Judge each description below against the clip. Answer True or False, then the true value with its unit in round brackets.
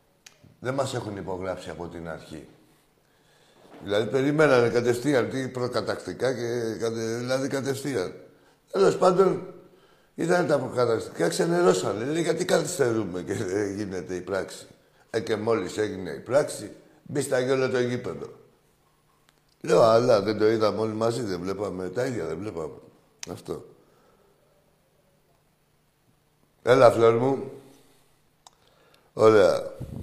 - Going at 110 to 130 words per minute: True (115 wpm)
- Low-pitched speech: True (120 Hz)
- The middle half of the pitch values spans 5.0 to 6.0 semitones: False (4.2 semitones)